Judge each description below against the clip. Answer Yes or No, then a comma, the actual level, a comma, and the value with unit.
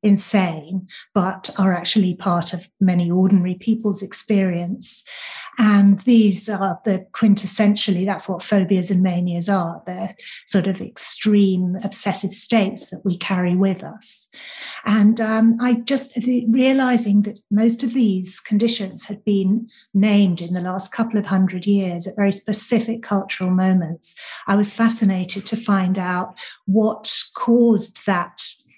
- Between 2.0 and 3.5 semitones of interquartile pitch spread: Yes, average, 2.9 semitones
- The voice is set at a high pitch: Yes, high, 200 Hz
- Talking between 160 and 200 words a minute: No, average, 140 wpm